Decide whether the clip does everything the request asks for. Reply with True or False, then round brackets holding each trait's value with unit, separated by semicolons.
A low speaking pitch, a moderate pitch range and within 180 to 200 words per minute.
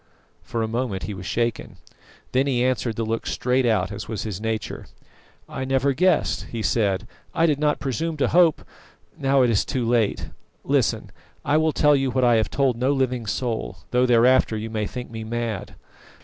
True (120 Hz; 3.2 semitones; 190 wpm)